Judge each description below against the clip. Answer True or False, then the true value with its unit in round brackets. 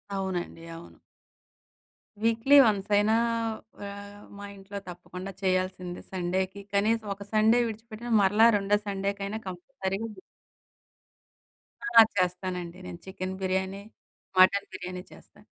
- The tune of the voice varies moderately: False (1.9 semitones)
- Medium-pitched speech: False (195 Hz)